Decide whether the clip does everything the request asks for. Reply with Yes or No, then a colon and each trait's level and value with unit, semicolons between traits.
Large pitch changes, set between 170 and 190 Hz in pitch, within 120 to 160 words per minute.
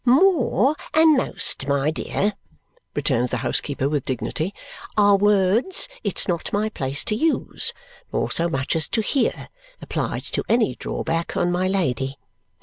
Yes: wide, 8.0 semitones; medium, 185 Hz; average, 145 wpm